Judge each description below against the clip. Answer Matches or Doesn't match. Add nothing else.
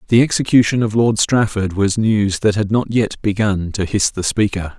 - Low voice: Matches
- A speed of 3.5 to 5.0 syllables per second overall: Matches